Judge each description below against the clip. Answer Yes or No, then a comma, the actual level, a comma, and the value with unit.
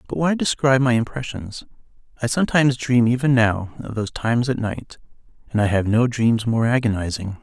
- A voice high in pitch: No, low, 120 Hz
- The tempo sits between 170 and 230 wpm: Yes, average, 180 wpm